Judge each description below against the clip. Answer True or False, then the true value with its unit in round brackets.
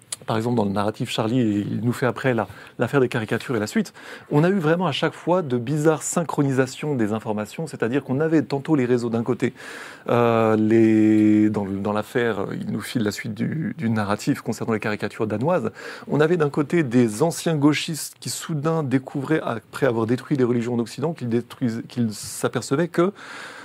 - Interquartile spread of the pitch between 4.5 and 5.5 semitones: True (5.2 semitones)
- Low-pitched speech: True (125 Hz)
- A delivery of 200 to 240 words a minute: False (190 wpm)